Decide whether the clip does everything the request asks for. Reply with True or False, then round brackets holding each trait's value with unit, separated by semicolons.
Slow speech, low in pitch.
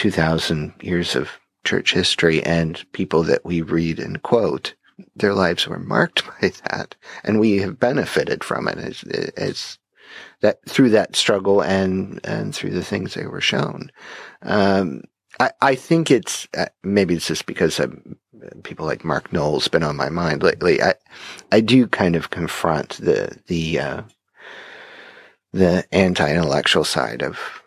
False (155 wpm; 95 Hz)